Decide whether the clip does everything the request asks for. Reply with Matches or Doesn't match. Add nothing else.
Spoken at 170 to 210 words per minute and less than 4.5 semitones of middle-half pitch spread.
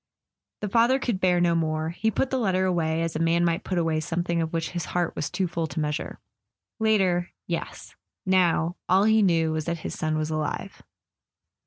Matches